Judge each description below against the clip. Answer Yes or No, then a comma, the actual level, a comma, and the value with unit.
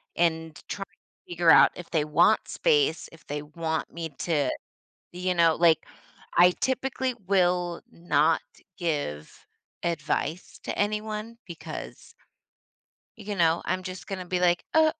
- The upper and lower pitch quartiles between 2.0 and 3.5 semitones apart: Yes, narrow, 2.5 semitones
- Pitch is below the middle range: No, medium, 170 Hz